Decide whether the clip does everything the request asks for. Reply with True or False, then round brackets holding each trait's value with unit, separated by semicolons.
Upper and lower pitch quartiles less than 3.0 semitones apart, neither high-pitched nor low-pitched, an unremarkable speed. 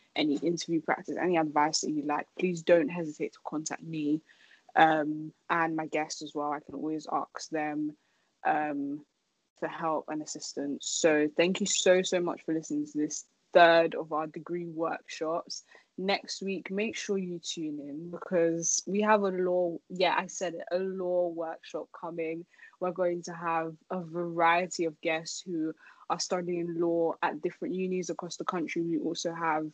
True (2.6 semitones; 170 Hz; 175 wpm)